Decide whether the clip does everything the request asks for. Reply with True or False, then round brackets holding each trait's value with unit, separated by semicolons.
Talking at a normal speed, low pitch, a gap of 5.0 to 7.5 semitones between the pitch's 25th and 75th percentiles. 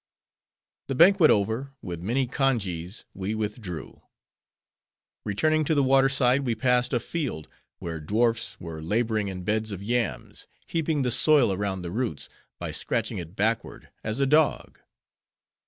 True (145 wpm; 115 Hz; 5.6 semitones)